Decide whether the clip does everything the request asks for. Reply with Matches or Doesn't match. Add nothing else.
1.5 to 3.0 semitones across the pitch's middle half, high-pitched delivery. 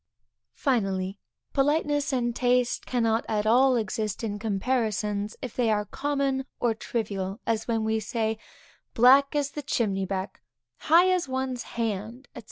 Doesn't match